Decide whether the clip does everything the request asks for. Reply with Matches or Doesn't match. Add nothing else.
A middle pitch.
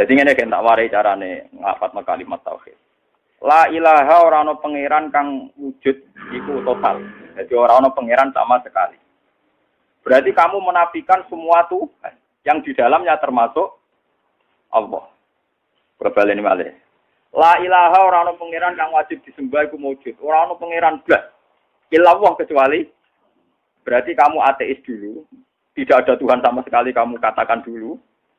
Matches